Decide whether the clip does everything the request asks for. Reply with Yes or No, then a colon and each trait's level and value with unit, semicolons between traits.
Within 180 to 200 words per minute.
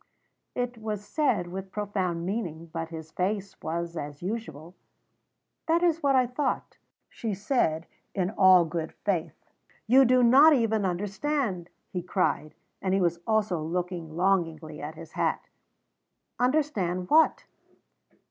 No: slow, 135 wpm